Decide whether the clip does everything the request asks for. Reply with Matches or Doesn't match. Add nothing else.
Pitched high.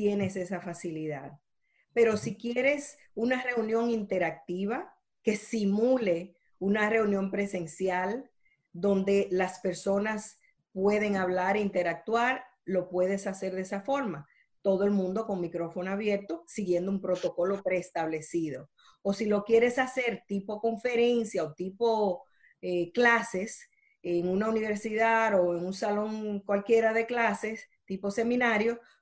Matches